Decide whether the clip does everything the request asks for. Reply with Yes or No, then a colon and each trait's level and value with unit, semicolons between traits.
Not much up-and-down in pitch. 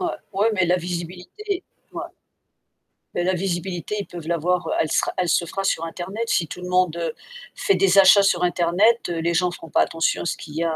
Yes: narrow, 2.2 semitones